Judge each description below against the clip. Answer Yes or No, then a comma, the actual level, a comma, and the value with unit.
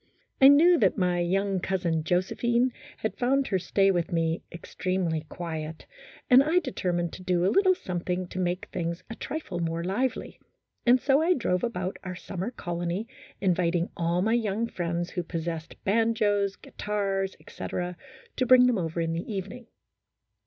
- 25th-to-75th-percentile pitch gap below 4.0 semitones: No, average, 4.8 semitones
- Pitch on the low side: No, medium, 185 Hz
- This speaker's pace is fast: No, average, 165 wpm